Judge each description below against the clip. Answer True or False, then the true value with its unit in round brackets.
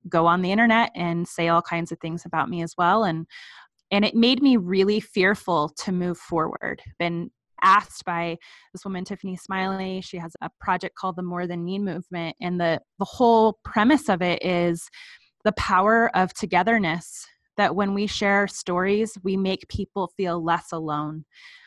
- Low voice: False (185 Hz)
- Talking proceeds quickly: False (175 wpm)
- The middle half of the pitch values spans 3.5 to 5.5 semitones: False (2.9 semitones)